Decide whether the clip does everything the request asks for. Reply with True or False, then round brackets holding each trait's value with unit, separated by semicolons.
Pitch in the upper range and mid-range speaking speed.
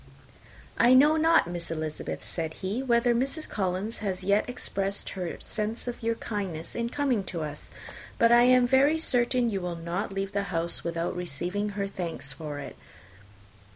True (200 Hz; 170 wpm)